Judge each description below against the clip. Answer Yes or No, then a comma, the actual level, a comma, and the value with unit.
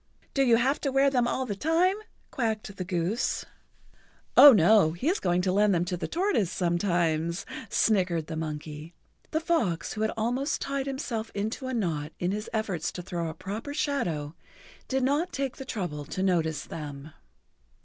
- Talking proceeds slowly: No, average, 180 wpm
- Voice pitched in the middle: No, high, 200 Hz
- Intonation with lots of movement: Yes, wide, 7.6 semitones